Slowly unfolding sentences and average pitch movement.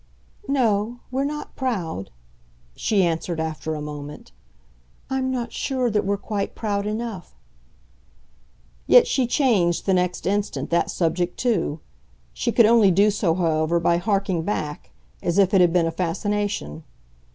No: average, 145 wpm; average, 4.6 semitones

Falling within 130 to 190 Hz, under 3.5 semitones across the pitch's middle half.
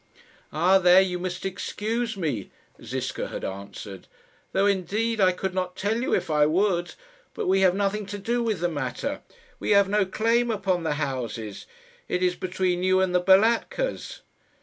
Yes: medium, 185 Hz; average, 2.7 semitones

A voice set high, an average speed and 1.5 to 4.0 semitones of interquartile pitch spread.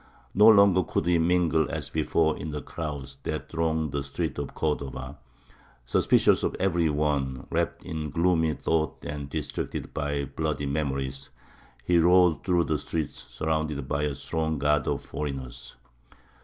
No: very low, 75 Hz; average, 150 wpm; narrow, 2.4 semitones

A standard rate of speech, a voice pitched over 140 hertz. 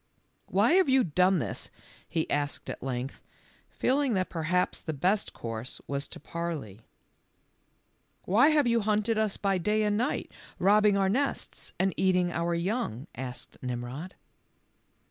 Yes: average, 145 wpm; medium, 185 Hz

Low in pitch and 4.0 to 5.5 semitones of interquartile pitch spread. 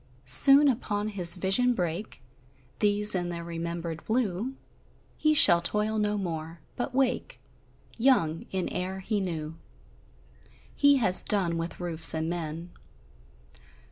No: medium, 185 Hz; average, 4.4 semitones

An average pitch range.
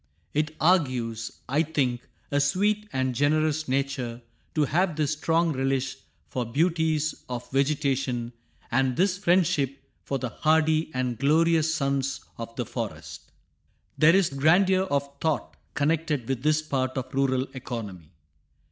Yes: average, 3.6 semitones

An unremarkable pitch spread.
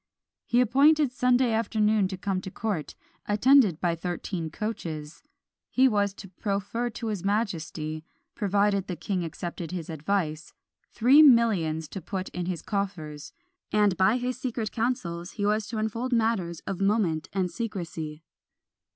Yes: average, 4.9 semitones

